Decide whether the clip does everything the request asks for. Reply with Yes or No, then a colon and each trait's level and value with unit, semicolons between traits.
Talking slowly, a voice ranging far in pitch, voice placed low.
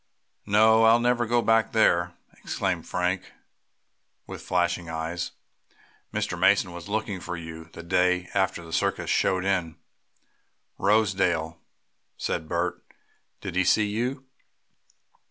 No: slow, 120 wpm; average, 4.1 semitones; very low, 90 Hz